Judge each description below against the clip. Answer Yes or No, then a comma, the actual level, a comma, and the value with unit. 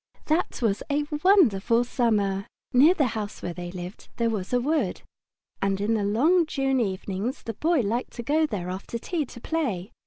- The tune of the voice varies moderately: No, wide, 6.4 semitones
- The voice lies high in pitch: Yes, high, 230 Hz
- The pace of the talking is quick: No, average, 185 wpm